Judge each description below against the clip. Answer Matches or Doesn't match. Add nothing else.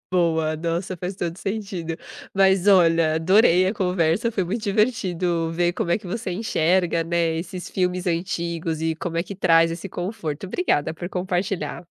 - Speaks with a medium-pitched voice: Matches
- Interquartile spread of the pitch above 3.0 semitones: Doesn't match